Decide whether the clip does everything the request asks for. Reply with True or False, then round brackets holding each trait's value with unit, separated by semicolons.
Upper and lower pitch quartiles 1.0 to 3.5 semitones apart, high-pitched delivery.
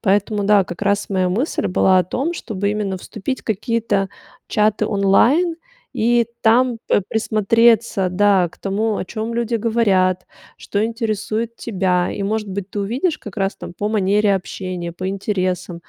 True (3.0 semitones; 205 Hz)